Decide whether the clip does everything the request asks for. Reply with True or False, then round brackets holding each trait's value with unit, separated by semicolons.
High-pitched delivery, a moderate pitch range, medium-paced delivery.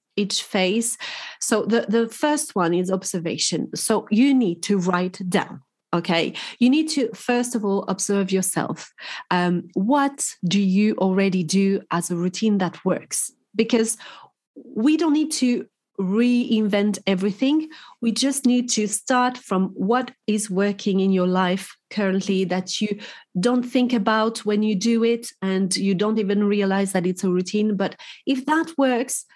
True (210 Hz; 4.3 semitones; 155 wpm)